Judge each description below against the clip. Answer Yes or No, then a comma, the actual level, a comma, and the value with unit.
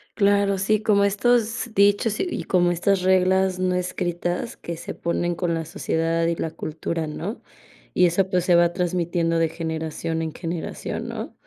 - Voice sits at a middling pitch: Yes, medium, 175 Hz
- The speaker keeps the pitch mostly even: No, average, 3.0 semitones